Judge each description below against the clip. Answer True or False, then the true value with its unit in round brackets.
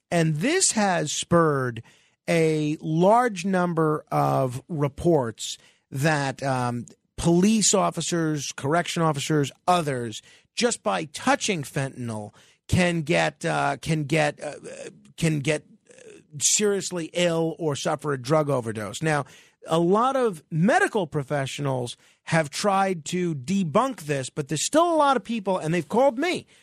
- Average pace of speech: False (130 wpm)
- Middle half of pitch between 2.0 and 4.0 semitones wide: False (5.0 semitones)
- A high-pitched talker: False (165 Hz)